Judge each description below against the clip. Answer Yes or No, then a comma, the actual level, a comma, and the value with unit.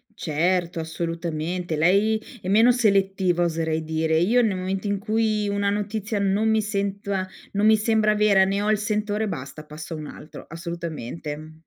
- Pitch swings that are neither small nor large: Yes, average, 4.2 semitones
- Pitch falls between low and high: No, high, 195 Hz